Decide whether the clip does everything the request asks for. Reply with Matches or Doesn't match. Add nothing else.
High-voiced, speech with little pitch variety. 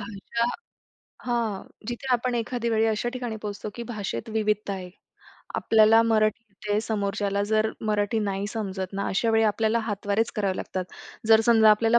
Matches